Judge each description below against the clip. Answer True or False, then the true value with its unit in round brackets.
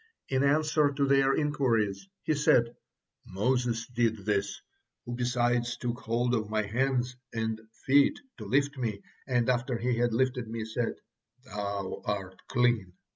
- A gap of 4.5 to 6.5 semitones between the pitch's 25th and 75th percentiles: False (2.9 semitones)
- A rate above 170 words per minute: False (145 wpm)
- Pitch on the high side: False (120 Hz)